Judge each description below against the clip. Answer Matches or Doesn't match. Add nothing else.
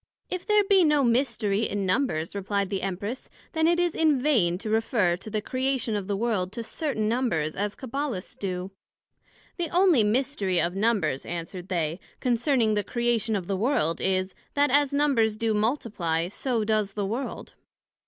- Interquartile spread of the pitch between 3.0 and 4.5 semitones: Doesn't match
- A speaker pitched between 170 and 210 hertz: Doesn't match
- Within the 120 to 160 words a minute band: Doesn't match